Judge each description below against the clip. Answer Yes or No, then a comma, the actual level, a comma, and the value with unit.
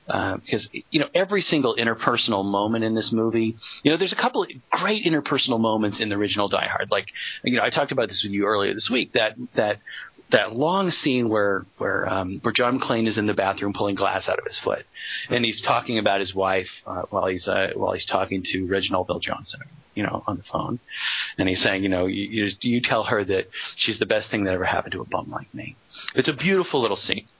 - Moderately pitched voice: No, low, 110 Hz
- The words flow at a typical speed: No, fast, 235 wpm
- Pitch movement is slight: No, average, 3.9 semitones